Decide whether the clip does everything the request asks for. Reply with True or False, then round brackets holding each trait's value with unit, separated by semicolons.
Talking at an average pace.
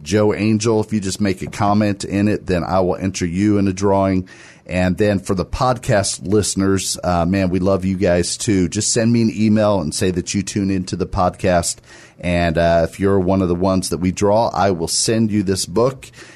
False (225 wpm)